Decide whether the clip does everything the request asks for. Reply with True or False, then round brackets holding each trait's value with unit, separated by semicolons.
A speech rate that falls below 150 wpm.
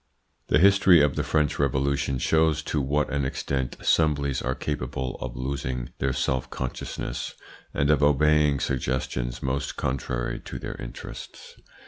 True (140 wpm)